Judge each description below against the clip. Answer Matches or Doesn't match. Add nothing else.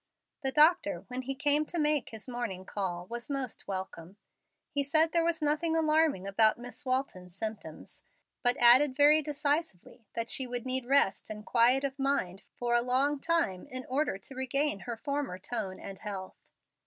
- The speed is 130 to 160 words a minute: Doesn't match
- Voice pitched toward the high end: Matches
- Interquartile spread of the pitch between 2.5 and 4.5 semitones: Doesn't match